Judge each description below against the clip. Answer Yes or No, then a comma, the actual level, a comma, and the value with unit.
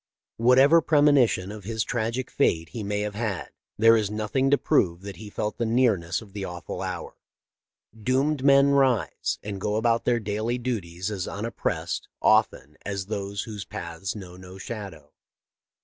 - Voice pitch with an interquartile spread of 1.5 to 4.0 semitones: Yes, average, 3.7 semitones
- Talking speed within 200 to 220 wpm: No, average, 165 wpm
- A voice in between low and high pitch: No, low, 105 Hz